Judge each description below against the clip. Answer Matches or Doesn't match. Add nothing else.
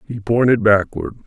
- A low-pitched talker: Matches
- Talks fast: Doesn't match